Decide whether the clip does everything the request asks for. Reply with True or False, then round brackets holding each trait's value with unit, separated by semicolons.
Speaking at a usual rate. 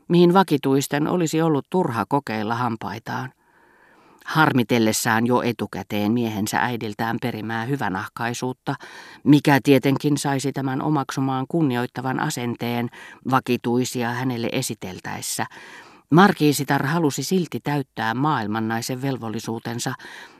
False (90 wpm)